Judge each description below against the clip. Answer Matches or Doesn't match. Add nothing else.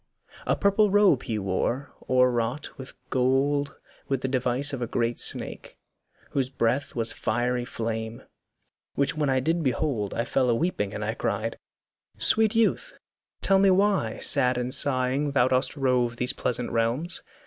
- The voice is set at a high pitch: Doesn't match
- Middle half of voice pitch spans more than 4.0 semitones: Doesn't match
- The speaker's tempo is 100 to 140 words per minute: Doesn't match